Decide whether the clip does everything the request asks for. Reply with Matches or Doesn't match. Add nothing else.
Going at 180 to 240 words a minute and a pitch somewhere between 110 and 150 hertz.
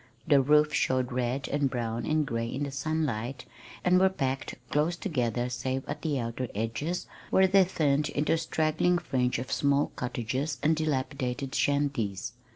Doesn't match